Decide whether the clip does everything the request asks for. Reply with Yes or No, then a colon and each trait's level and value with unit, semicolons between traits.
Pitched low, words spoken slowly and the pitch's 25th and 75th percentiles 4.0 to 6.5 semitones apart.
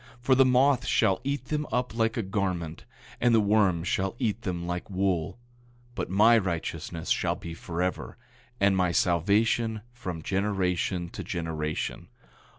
No: very low, 95 Hz; average, 155 wpm; average, 4.6 semitones